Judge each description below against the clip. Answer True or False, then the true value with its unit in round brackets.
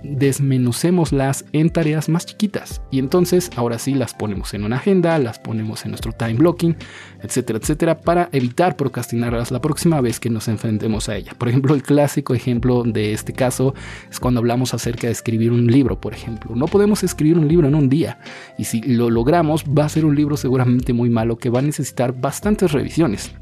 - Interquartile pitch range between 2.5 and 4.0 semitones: False (4.7 semitones)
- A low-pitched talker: True (130 Hz)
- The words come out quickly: True (200 wpm)